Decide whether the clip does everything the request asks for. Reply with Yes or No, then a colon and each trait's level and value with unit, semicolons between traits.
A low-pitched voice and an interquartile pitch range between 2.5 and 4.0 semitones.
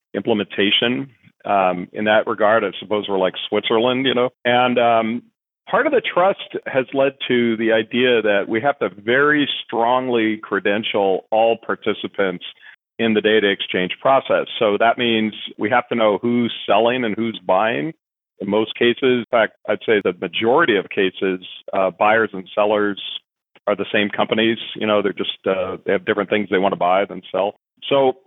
Yes: low, 115 Hz; average, 2.8 semitones